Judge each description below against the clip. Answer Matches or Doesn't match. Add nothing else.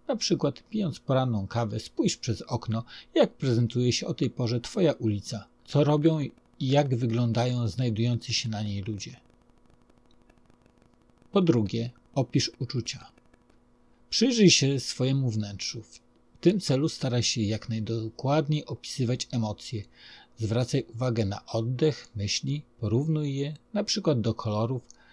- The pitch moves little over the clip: Doesn't match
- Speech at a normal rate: Matches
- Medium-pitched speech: Doesn't match